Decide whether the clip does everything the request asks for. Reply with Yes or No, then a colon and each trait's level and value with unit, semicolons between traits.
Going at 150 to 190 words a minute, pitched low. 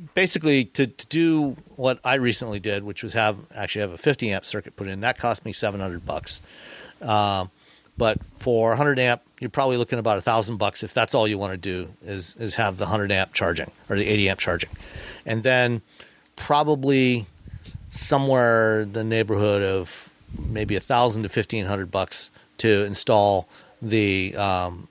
Yes: average, 180 wpm; low, 110 Hz